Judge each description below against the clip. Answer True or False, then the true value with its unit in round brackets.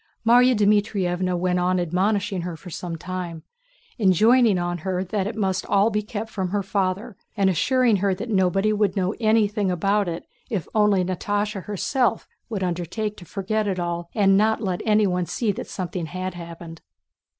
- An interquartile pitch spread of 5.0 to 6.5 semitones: False (2.8 semitones)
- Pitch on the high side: True (195 Hz)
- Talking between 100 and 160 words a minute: False (170 wpm)